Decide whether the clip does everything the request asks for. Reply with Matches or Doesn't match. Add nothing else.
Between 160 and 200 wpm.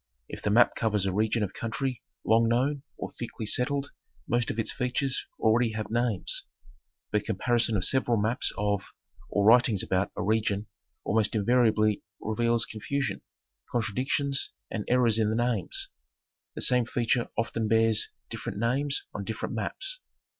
Doesn't match